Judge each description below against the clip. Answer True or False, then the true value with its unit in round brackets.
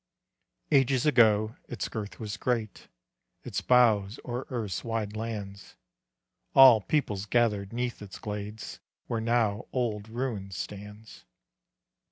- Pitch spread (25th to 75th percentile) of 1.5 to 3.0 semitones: True (2.7 semitones)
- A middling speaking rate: False (115 wpm)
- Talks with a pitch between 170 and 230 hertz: False (110 Hz)